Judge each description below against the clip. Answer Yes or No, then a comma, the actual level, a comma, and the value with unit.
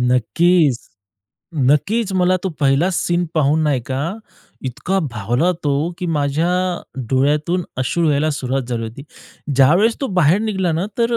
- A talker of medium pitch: Yes, medium, 155 Hz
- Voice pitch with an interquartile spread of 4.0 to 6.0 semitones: Yes, average, 4.8 semitones